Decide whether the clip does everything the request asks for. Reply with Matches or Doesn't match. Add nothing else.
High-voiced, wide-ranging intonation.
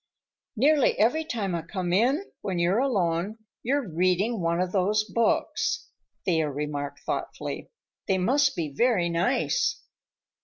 Matches